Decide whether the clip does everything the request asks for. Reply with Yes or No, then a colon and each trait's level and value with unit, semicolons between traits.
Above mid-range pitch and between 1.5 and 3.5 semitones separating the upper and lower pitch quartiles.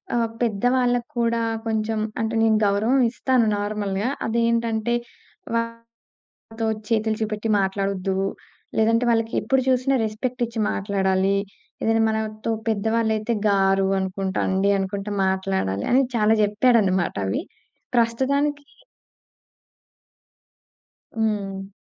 Yes: high, 220 Hz; average, 2.8 semitones